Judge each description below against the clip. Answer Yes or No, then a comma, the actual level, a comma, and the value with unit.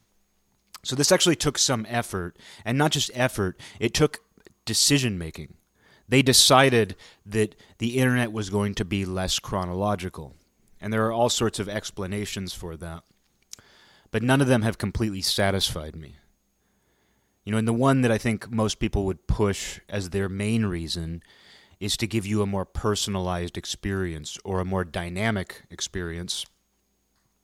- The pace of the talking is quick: No, average, 155 wpm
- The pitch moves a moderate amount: Yes, average, 4.0 semitones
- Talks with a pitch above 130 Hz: No, low, 100 Hz